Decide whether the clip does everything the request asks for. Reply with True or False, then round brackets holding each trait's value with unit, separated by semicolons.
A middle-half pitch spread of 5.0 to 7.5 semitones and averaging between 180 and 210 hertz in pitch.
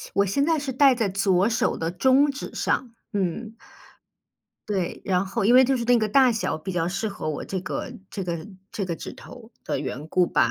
True (5.4 semitones; 200 Hz)